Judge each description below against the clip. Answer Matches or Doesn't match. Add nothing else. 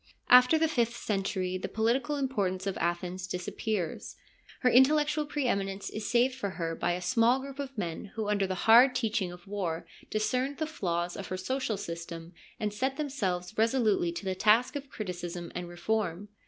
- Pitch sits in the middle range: Doesn't match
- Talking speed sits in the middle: Matches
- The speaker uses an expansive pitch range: Matches